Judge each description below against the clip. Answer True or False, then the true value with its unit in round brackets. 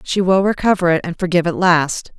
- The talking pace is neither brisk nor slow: False (220 wpm)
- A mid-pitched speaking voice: True (175 Hz)